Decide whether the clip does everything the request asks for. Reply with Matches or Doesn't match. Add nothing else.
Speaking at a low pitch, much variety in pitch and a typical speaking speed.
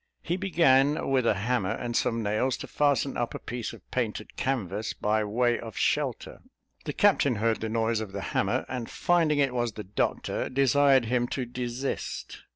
Doesn't match